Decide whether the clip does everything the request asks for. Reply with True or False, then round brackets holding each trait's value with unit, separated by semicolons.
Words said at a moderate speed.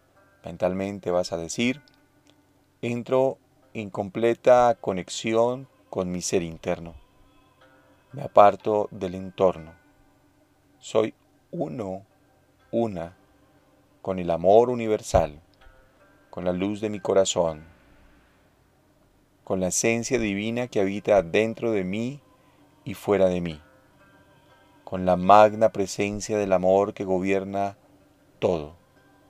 False (105 wpm)